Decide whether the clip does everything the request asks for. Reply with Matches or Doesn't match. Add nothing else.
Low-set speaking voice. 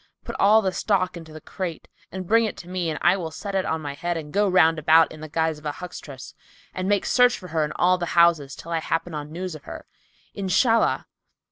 Doesn't match